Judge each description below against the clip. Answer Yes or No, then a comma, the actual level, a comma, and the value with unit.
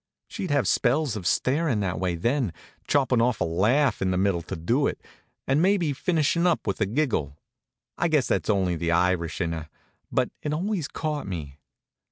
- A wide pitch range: Yes, wide, 8.7 semitones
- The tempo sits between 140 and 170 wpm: No, average, 190 wpm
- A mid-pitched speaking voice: No, low, 115 Hz